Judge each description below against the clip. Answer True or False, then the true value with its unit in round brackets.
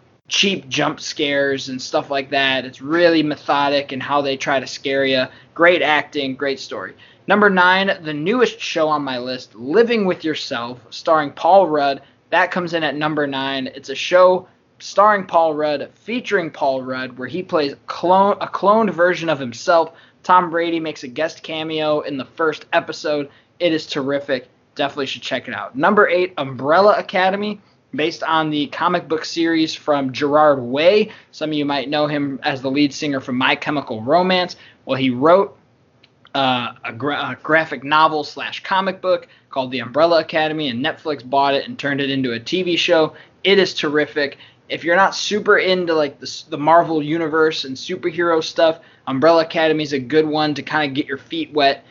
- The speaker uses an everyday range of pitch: True (3.5 semitones)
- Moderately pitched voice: True (150 Hz)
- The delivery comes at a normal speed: True (185 wpm)